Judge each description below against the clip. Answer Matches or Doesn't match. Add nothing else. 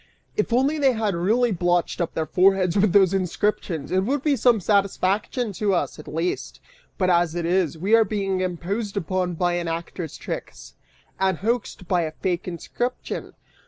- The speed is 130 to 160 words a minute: Doesn't match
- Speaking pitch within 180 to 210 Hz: Matches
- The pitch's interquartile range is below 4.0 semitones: Matches